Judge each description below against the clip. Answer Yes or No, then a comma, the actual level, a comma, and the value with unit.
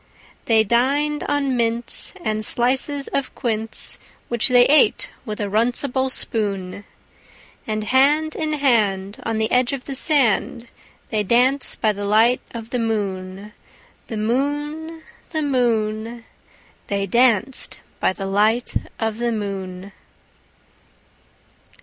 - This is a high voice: Yes, high, 235 Hz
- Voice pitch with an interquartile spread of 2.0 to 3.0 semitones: No, average, 3.8 semitones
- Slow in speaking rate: Yes, slow, 125 wpm